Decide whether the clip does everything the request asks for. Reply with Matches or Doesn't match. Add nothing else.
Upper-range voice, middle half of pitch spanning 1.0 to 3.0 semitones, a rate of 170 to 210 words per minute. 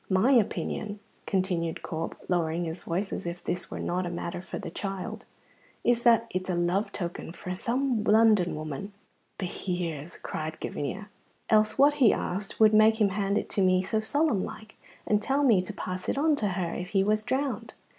Doesn't match